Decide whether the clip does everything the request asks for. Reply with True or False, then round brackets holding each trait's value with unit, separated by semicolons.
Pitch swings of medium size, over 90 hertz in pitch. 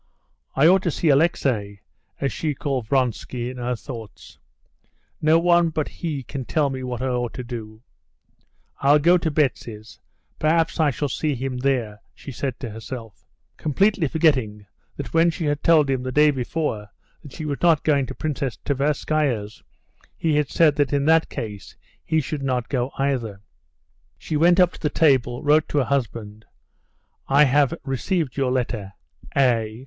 True (4.0 semitones; 135 Hz)